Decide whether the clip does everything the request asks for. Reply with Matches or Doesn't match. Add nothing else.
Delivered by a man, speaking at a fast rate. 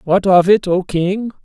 Matches